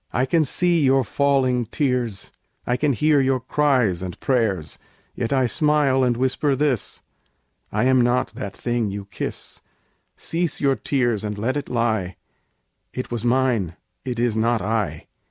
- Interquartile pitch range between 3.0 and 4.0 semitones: Yes, average, 3.4 semitones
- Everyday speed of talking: Yes, average, 155 wpm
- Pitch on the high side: No, low, 125 Hz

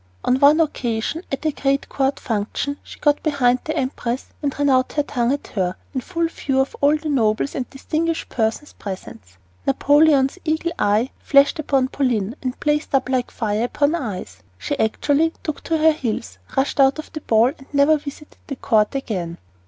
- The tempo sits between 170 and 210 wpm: Yes, average, 185 wpm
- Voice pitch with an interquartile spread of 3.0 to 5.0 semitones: Yes, average, 4.2 semitones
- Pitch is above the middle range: Yes, very high, 275 Hz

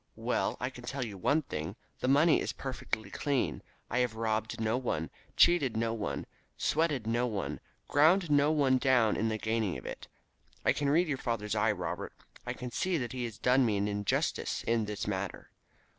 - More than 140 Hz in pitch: No, low, 120 Hz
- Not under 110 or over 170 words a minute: No, average, 195 wpm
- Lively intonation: No, average, 4.3 semitones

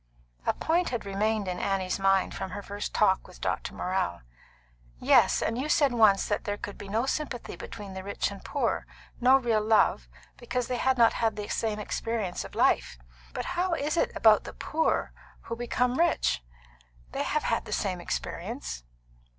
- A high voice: Yes, high, 215 Hz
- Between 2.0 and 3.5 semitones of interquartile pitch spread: No, average, 4.2 semitones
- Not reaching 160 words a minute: No, average, 185 wpm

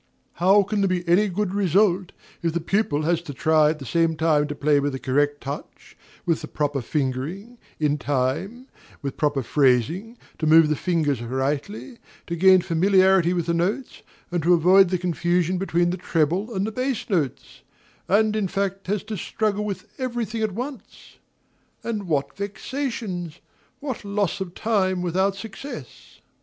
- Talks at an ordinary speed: Yes, average, 170 wpm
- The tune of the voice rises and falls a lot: No, average, 4.8 semitones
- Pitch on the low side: No, medium, 180 Hz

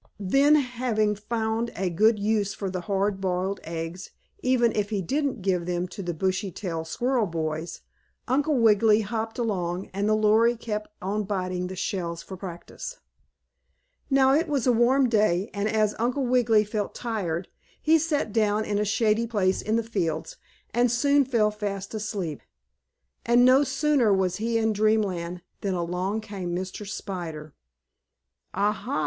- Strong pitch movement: No, average, 4.0 semitones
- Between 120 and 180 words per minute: Yes, average, 160 wpm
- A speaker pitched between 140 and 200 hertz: No, high, 210 Hz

